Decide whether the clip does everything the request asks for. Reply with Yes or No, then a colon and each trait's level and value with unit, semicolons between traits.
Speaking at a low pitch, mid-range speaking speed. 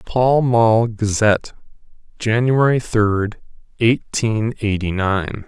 No: low, 110 Hz; slow, 90 wpm